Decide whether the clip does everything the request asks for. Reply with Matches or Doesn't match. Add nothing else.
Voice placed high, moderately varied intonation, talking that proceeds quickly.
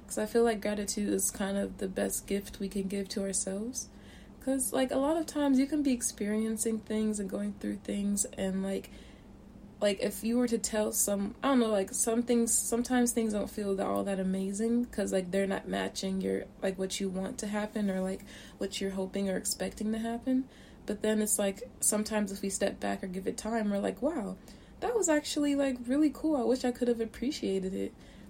Matches